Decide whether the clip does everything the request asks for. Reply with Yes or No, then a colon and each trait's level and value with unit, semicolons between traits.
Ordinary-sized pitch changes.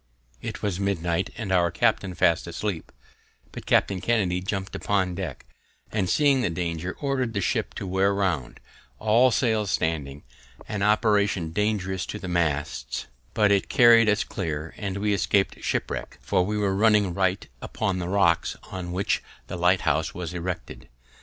Yes: average, 3.1 semitones